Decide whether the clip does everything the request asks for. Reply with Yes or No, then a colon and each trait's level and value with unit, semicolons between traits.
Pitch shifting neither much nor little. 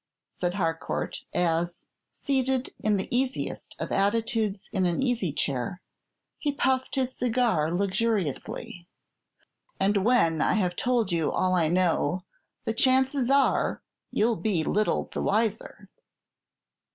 No: wide, 5.7 semitones